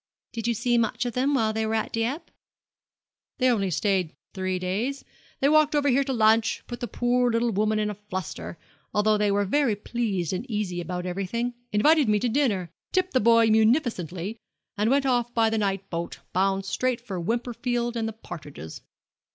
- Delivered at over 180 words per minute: Yes, average, 190 wpm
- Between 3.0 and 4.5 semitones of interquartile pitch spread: Yes, average, 3.7 semitones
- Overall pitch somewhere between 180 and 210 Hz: No, high, 220 Hz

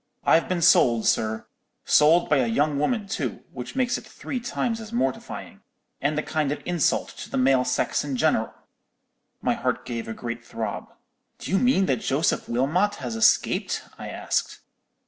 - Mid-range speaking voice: Yes, medium, 145 Hz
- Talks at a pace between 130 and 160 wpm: No, average, 170 wpm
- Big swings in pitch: Yes, wide, 6.7 semitones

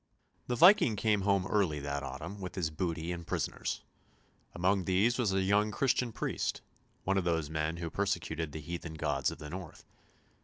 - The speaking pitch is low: Yes, very low, 90 Hz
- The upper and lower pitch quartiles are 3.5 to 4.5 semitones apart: Yes, average, 4.1 semitones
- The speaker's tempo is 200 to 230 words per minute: No, average, 180 wpm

